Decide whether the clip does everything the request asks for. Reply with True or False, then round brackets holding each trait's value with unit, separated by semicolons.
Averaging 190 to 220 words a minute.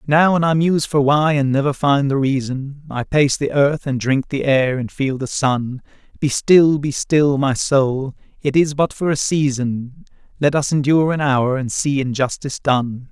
True (200 wpm)